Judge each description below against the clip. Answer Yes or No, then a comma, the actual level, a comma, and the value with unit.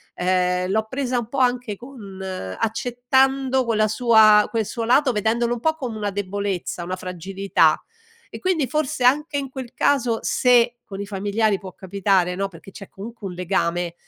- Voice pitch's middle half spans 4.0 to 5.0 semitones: Yes, average, 4.5 semitones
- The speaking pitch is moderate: No, high, 215 Hz